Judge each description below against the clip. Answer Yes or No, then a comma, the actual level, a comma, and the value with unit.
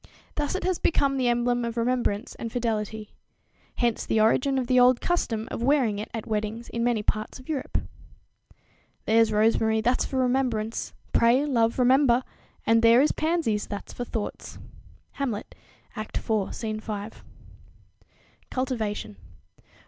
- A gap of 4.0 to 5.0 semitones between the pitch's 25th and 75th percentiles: No, average, 2.9 semitones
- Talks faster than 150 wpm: No, average, 145 wpm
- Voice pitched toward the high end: Yes, high, 235 Hz